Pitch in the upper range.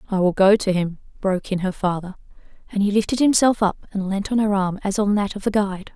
Yes: high, 200 Hz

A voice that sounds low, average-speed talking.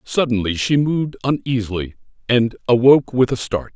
Yes: low, 120 Hz; average, 145 wpm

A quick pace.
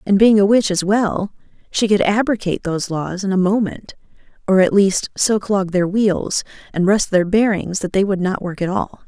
Yes: fast, 210 wpm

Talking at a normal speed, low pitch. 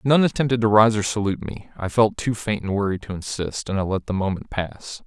No: fast, 250 wpm; low, 105 Hz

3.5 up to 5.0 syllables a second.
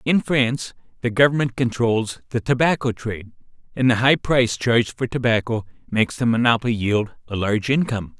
No: 5.8 syllables/s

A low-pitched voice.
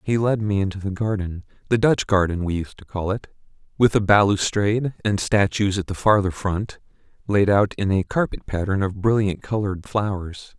Yes: low, 100 Hz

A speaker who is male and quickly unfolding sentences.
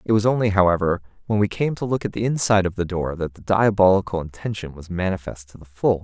Yes: male; fast, 240 wpm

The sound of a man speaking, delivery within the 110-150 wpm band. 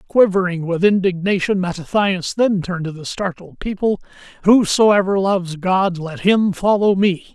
Yes: male; average, 140 wpm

